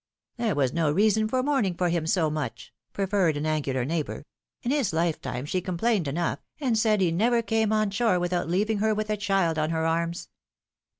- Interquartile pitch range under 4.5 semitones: No, average, 5.1 semitones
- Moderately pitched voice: Yes, medium, 180 Hz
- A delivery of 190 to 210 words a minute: Yes, average, 200 wpm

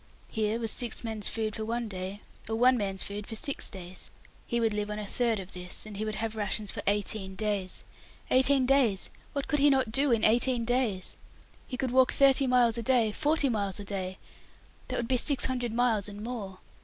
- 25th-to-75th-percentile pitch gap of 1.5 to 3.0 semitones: No, average, 3.4 semitones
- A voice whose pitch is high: Yes, high, 225 Hz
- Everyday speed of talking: No, fast, 215 wpm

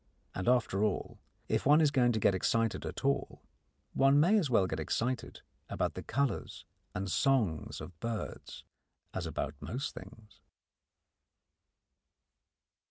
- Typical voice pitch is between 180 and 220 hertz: No, low, 115 Hz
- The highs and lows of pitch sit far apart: Yes, wide, 5.8 semitones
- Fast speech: No, slow, 135 wpm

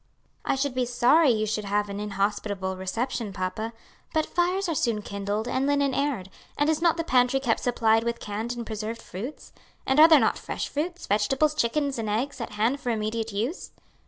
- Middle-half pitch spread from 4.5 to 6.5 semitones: Yes, average, 5.1 semitones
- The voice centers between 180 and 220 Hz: No, high, 235 Hz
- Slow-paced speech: No, average, 195 wpm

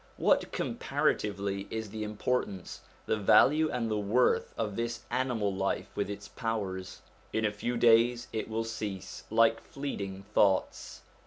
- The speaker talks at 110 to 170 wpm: Yes, average, 145 wpm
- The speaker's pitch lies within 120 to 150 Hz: No, low, 110 Hz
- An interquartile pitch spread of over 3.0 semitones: No, narrow, 2.6 semitones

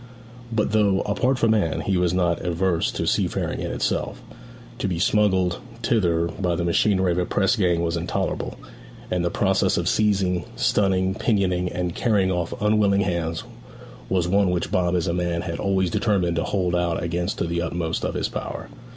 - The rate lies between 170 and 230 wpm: Yes, average, 185 wpm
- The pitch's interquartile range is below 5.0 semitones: Yes, narrow, 2.5 semitones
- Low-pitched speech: Yes, very low, 90 Hz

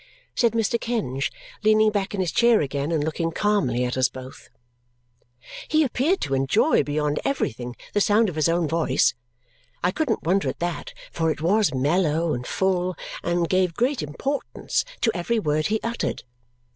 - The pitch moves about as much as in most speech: No, wide, 6.4 semitones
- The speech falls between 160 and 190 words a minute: Yes, average, 170 wpm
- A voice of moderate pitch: Yes, medium, 175 Hz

